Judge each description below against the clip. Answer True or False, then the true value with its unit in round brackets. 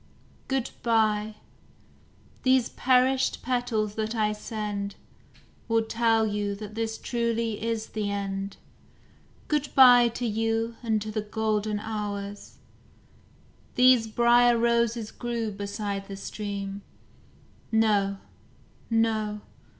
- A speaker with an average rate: False (105 wpm)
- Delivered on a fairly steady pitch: True (2.1 semitones)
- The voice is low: False (220 Hz)